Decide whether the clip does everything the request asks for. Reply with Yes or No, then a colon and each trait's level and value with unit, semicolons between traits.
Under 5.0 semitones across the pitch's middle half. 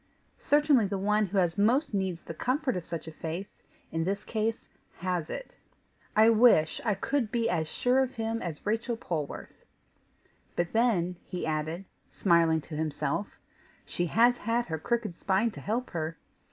No: wide, 5.5 semitones